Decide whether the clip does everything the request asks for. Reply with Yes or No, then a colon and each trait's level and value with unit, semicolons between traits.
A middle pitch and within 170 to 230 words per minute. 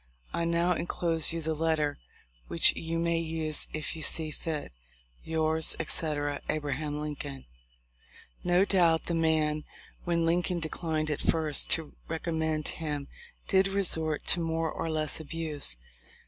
No: medium, 160 Hz; average, 140 wpm